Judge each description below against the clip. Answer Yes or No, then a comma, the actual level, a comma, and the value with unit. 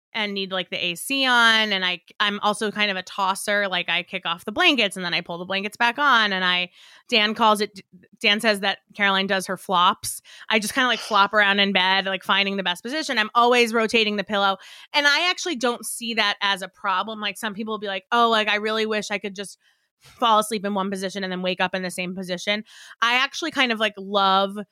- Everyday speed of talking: No, fast, 245 wpm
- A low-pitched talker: No, high, 205 Hz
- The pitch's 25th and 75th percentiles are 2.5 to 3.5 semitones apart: Yes, average, 2.8 semitones